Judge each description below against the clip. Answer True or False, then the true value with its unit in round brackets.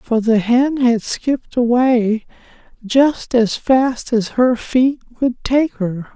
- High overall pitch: True (240 Hz)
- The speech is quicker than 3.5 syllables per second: False (3.2 syllables/s)